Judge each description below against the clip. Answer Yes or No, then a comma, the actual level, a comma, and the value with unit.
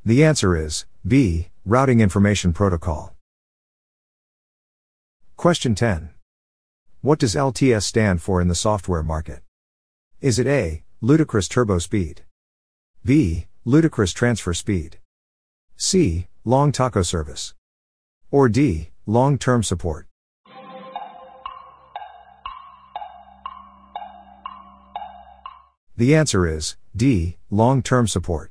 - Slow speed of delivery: Yes, slow, 95 wpm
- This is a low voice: Yes, low, 105 Hz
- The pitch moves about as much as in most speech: No, wide, 9.0 semitones